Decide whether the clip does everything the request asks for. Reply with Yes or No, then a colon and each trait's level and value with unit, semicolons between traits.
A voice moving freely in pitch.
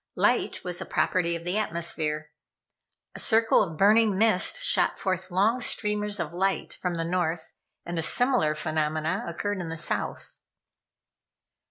No: average, 4.1 semitones